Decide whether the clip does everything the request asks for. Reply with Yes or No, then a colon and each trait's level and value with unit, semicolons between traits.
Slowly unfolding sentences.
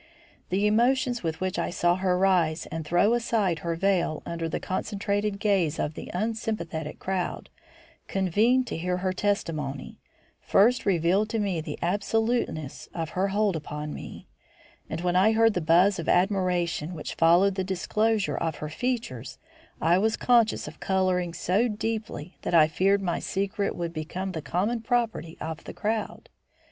No: average, 160 wpm